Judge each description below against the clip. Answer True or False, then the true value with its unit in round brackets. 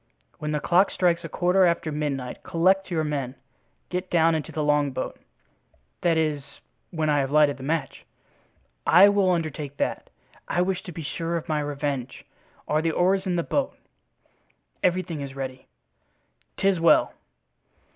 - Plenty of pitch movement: False (3.4 semitones)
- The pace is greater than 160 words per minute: False (155 wpm)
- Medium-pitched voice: True (160 Hz)